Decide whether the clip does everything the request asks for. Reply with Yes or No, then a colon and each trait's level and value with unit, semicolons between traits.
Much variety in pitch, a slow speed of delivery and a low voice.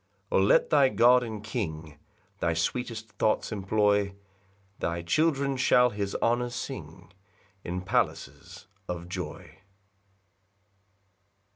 Yes: wide, 5.7 semitones; slow, 110 wpm; low, 105 Hz